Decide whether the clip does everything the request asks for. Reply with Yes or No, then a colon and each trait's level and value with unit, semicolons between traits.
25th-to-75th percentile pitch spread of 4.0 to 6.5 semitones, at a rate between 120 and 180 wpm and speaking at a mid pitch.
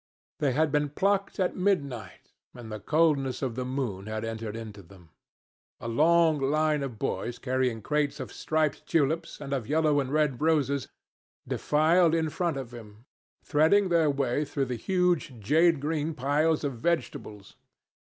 Yes: average, 4.6 semitones; average, 160 wpm; medium, 145 Hz